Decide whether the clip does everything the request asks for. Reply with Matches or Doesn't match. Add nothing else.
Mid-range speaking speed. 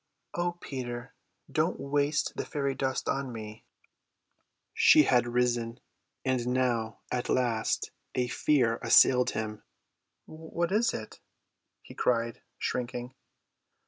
Doesn't match